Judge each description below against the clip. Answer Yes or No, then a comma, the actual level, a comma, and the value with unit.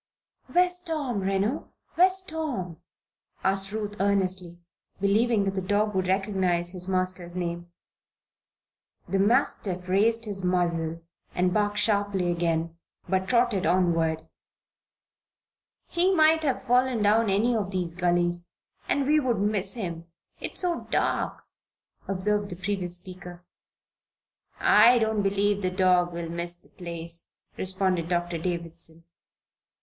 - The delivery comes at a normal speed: No, slow, 125 wpm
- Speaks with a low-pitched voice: No, high, 190 Hz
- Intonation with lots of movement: No, average, 3.5 semitones